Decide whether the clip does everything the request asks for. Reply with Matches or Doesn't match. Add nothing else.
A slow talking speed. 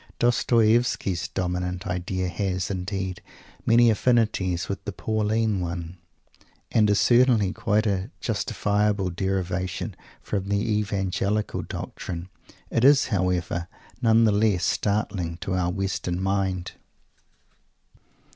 Matches